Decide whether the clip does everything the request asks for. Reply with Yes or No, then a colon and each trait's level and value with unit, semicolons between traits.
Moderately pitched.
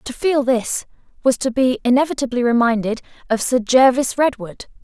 No: very high, 250 Hz